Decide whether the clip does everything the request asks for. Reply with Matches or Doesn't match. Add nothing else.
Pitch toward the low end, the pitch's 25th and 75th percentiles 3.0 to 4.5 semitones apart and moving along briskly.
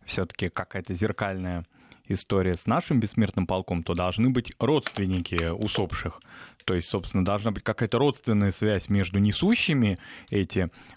Doesn't match